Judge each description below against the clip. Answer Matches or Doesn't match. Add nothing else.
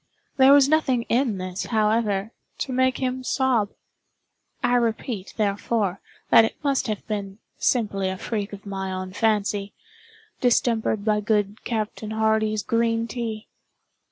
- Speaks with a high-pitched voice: Matches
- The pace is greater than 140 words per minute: Doesn't match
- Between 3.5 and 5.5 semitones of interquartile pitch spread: Doesn't match